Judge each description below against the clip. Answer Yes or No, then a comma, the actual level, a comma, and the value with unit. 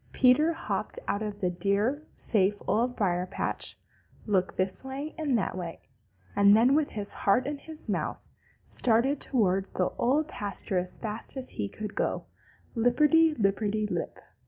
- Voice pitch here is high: Yes, high, 220 Hz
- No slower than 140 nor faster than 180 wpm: Yes, average, 160 wpm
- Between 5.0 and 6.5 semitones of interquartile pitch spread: Yes, average, 5.3 semitones